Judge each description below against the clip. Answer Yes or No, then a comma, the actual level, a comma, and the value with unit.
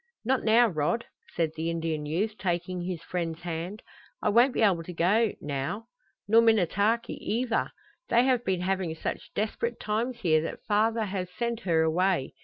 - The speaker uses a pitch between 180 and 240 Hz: Yes, high, 190 Hz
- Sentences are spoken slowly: No, average, 170 wpm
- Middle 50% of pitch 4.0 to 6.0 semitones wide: Yes, average, 5.3 semitones